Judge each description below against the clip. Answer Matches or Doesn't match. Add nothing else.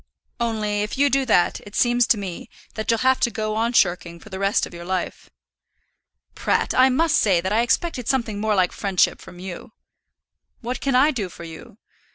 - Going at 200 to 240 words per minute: Matches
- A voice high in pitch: Matches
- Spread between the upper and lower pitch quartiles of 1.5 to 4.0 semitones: Doesn't match